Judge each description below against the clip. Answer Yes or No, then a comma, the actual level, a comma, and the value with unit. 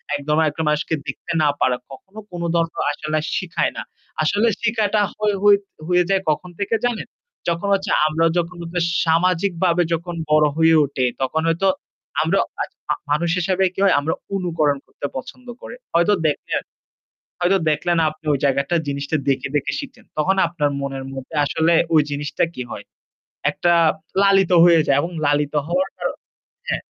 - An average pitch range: Yes, average, 3.7 semitones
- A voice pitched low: No, medium, 165 Hz